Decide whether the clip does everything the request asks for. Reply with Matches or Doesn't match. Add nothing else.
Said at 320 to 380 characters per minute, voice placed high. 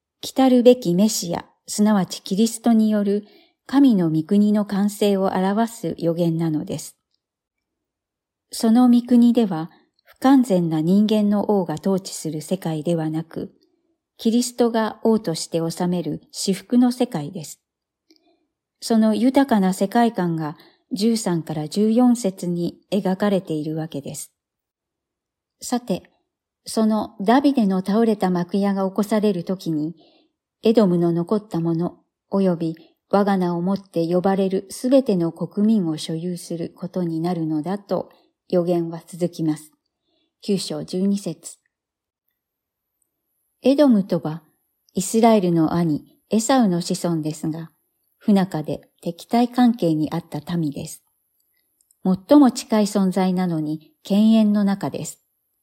Doesn't match